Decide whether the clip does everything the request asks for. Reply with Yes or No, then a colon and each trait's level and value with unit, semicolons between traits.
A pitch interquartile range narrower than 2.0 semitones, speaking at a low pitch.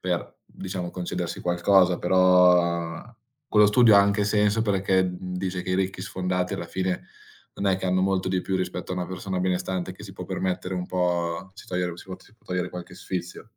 Yes: narrow, 1.0 semitones; very low, 90 Hz